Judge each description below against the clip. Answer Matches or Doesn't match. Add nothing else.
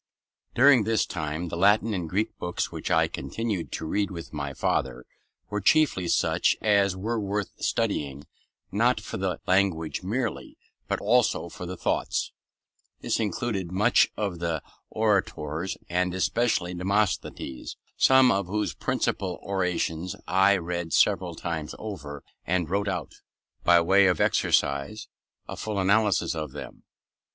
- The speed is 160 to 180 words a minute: Doesn't match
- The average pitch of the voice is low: Matches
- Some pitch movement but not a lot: Matches